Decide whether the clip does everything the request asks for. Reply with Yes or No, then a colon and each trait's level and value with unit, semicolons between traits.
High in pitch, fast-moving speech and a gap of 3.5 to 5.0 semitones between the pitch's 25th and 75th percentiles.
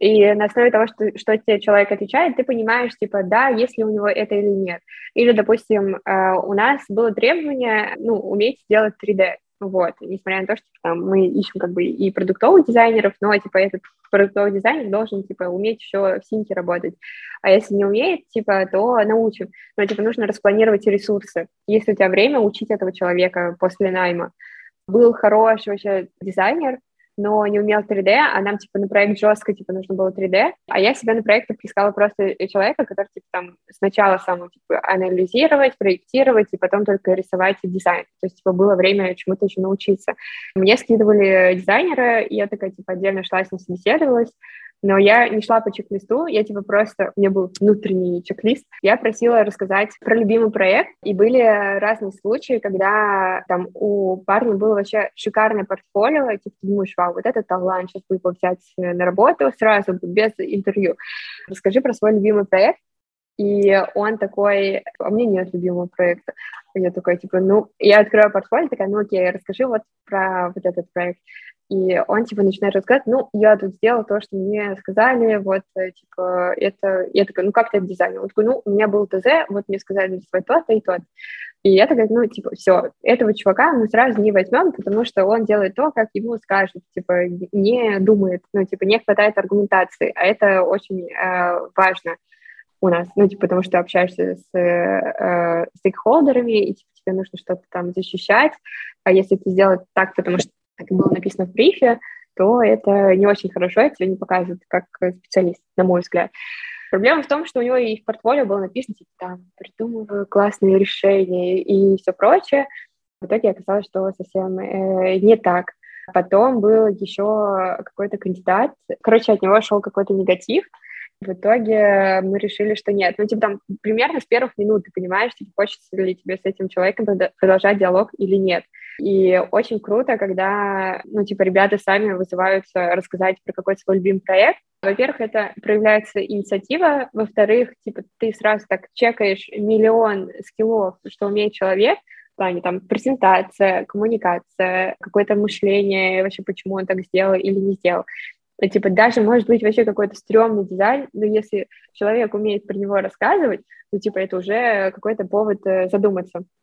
No: high, 200 Hz; fast, 175 wpm; narrow, 2.4 semitones